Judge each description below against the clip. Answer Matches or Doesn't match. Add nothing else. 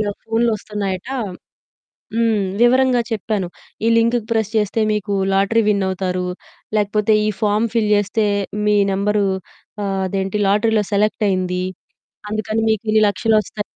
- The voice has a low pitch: Doesn't match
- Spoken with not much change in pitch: Matches